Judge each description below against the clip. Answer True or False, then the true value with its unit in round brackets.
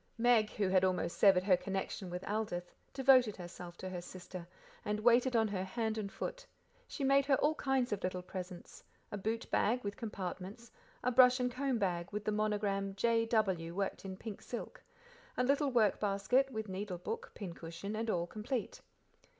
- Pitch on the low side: False (210 Hz)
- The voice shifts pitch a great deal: False (4.4 semitones)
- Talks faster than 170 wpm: True (180 wpm)